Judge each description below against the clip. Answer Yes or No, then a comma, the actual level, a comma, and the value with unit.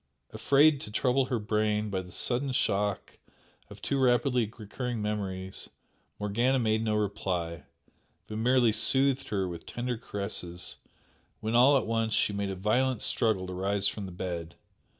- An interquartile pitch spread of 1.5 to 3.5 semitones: No, average, 4.0 semitones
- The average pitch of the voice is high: No, low, 105 Hz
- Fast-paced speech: No, average, 155 wpm